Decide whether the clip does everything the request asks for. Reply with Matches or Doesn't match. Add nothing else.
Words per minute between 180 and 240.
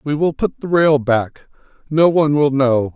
Matches